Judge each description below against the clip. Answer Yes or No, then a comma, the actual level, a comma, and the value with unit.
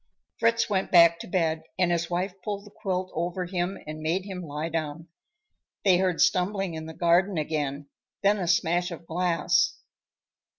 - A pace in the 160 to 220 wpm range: Yes, average, 170 wpm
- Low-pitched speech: No, medium, 175 Hz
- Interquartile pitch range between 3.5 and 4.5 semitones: No, narrow, 2.4 semitones